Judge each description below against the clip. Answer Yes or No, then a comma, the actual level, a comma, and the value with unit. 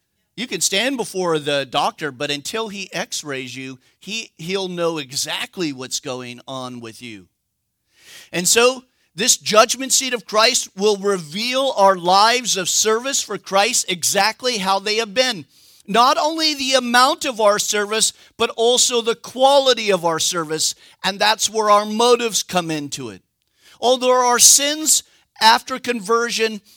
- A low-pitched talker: No, high, 210 Hz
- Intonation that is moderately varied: No, wide, 6.2 semitones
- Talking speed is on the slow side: No, average, 150 wpm